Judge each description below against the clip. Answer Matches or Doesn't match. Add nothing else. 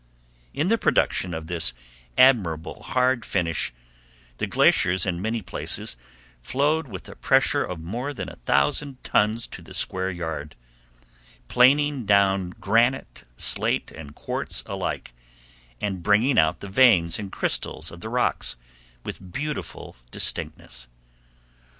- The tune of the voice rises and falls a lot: Matches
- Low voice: Matches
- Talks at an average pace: Doesn't match